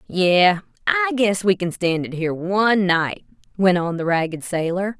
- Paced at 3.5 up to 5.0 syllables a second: Yes, 4.8 syllables/s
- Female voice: Yes, female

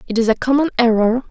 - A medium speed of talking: No, fast, 230 wpm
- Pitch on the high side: Yes, high, 240 Hz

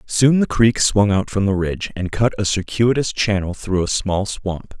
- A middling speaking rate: No, fast, 215 wpm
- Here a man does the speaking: Yes, male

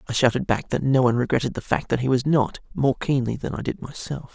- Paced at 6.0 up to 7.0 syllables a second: Yes, 6.2 syllables/s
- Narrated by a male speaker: Yes, male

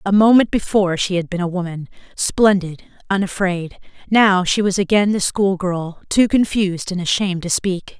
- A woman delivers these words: Yes, female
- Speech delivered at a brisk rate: No, average, 165 wpm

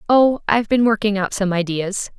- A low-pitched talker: No, high, 210 Hz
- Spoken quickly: No, average, 165 wpm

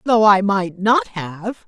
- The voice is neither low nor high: No, high, 210 Hz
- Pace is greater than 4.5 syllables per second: No, 4.2 syllables/s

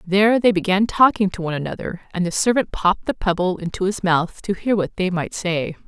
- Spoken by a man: No, female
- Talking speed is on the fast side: Yes, fast, 225 wpm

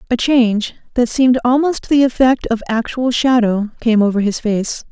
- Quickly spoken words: No, average, 170 wpm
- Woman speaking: Yes, female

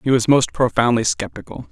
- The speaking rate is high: No, average, 175 wpm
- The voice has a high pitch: No, low, 125 Hz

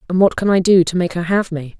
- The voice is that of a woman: Yes, female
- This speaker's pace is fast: Yes, fast, 335 wpm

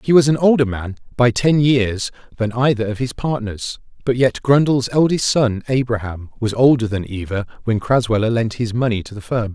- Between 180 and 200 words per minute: Yes, average, 195 wpm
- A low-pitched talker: Yes, low, 120 Hz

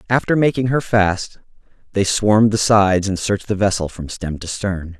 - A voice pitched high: No, low, 100 Hz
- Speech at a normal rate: Yes, average, 190 wpm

